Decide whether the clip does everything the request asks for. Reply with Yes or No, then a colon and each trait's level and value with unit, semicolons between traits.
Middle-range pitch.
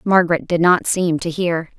Yes: medium, 175 Hz